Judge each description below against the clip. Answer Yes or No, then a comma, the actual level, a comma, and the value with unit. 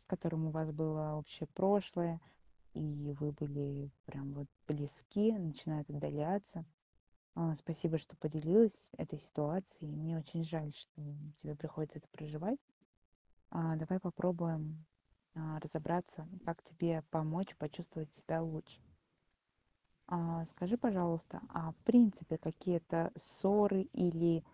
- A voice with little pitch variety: Yes, narrow, 2.2 semitones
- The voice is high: No, medium, 160 Hz